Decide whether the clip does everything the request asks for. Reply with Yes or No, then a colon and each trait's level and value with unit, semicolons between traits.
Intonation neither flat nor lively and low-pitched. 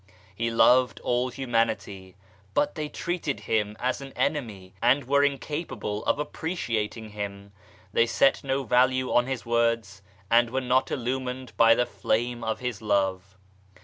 Yes: average, 3.4 semitones; low, 120 Hz